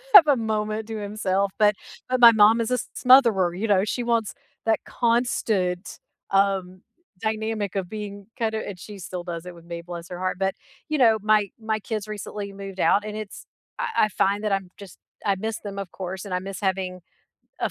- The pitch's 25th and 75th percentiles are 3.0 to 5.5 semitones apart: No, narrow, 2.6 semitones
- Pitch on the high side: Yes, high, 205 Hz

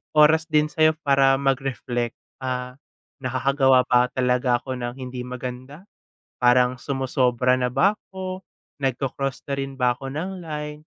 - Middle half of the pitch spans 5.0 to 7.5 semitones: No, average, 2.8 semitones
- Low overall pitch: Yes, low, 130 Hz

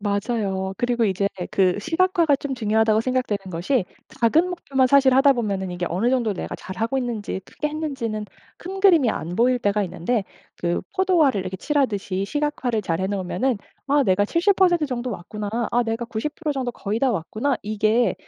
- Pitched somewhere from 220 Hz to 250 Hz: Yes, high, 235 Hz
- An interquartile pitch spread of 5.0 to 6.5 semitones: Yes, wide, 5.4 semitones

